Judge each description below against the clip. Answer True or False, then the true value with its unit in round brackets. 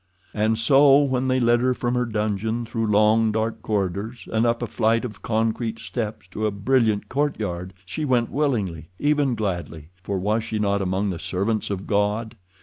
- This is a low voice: True (110 Hz)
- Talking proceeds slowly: False (175 wpm)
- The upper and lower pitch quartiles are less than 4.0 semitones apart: True (2.9 semitones)